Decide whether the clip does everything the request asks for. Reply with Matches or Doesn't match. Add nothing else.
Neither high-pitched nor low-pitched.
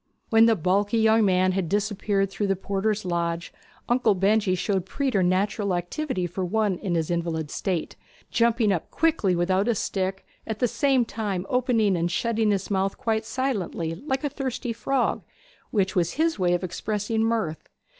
Doesn't match